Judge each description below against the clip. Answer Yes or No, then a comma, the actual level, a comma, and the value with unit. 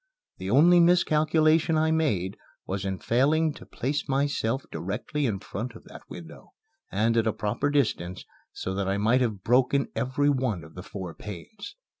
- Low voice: Yes, low, 125 Hz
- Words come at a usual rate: Yes, average, 170 wpm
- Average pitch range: No, wide, 6.9 semitones